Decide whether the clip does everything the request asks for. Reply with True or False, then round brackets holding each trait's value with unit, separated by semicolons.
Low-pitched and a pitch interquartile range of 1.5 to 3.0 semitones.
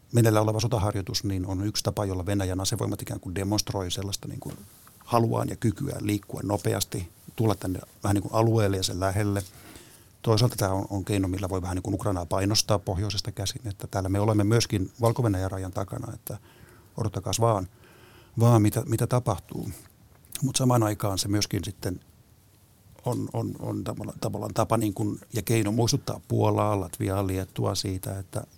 True (105 Hz; 2.7 semitones)